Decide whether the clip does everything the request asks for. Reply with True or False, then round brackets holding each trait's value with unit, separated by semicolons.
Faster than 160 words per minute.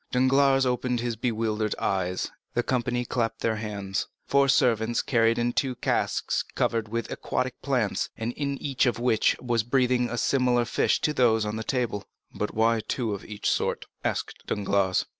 True (175 wpm)